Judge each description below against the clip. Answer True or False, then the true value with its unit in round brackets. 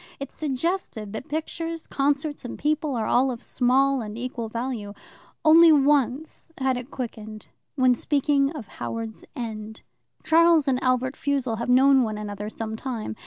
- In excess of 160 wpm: False (155 wpm)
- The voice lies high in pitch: True (255 Hz)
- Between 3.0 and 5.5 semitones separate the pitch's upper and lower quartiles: True (4.1 semitones)